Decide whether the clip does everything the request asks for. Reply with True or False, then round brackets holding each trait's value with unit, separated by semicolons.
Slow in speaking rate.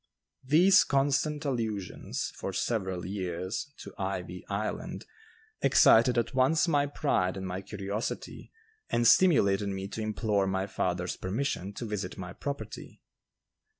True (125 wpm)